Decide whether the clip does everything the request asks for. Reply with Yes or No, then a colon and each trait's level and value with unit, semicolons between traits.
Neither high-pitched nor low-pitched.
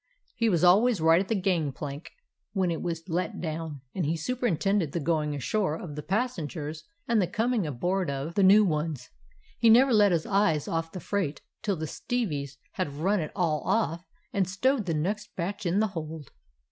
Yes: medium, 175 Hz